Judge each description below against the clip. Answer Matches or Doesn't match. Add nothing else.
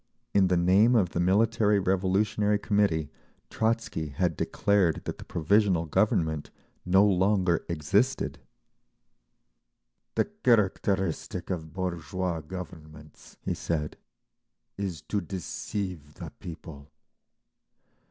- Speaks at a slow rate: Matches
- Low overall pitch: Matches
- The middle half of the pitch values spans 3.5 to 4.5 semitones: Matches